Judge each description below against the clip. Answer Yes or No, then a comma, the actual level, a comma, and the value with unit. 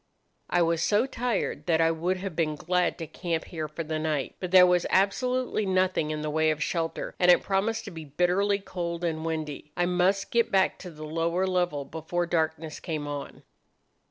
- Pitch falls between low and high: Yes, medium, 175 Hz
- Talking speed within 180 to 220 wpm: Yes, average, 200 wpm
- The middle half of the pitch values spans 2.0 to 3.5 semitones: Yes, average, 2.9 semitones